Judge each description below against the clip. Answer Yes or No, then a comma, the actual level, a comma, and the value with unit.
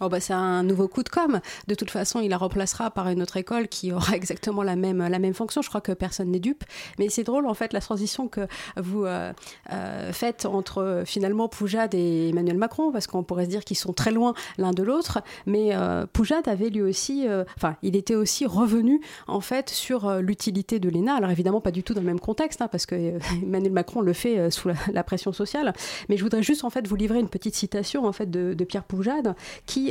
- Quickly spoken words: Yes, fast, 245 wpm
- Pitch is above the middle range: Yes, high, 200 Hz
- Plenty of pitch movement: No, average, 3.5 semitones